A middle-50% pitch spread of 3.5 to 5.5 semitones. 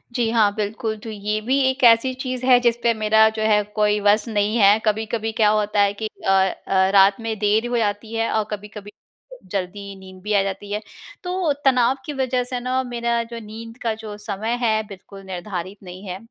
No: narrow, 2.5 semitones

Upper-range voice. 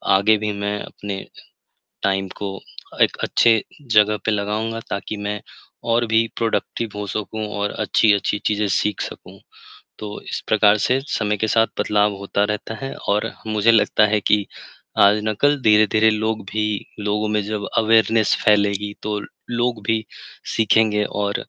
No: low, 105 Hz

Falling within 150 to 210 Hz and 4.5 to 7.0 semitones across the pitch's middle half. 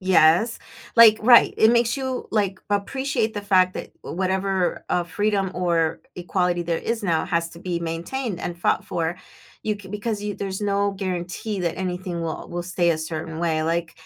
No: medium, 185 Hz; average, 3.4 semitones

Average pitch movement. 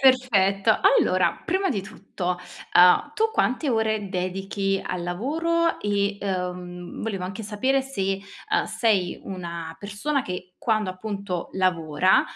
Yes: average, 3.7 semitones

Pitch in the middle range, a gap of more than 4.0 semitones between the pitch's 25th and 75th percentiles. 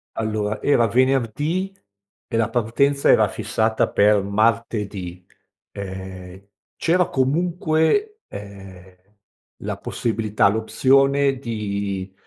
No: low, 110 Hz; wide, 5.4 semitones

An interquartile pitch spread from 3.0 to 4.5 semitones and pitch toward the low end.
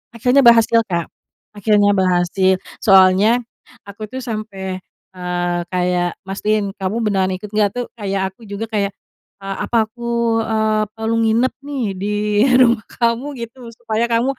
No: average, 3.3 semitones; high, 215 Hz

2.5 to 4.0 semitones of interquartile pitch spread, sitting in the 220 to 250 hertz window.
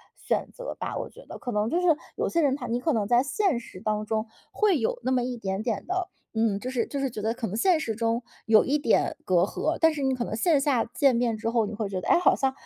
No: average, 4.7 semitones; high, 240 Hz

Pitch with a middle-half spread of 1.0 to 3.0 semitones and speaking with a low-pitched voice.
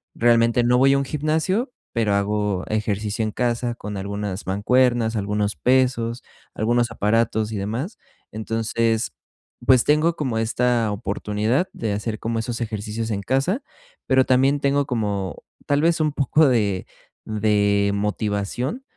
No: average, 3.7 semitones; low, 115 Hz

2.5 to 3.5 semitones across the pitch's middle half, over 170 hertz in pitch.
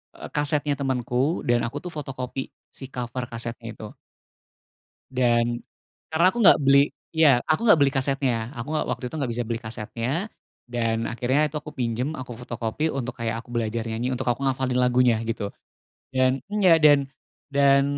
No: average, 2.9 semitones; low, 125 Hz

